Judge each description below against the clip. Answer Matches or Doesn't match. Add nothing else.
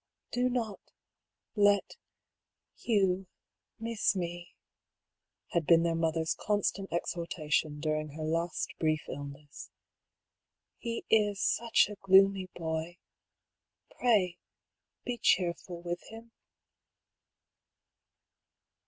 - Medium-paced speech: Doesn't match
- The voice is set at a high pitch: Doesn't match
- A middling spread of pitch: Matches